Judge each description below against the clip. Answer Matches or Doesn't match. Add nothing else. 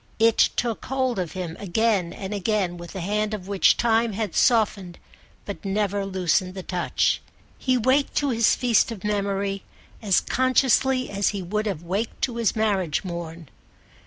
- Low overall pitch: Doesn't match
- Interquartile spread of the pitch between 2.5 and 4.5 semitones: Matches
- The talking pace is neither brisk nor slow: Matches